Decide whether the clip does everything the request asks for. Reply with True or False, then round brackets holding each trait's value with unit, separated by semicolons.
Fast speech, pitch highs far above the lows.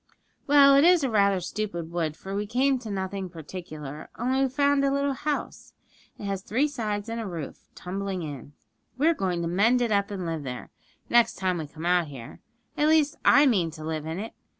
True (210 wpm; 7.3 semitones)